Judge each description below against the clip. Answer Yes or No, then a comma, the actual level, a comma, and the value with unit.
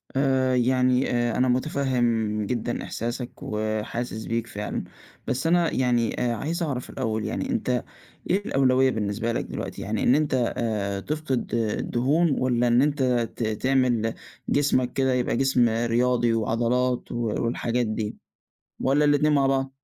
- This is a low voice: Yes, low, 125 Hz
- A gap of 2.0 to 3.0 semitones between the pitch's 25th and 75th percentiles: Yes, average, 2.7 semitones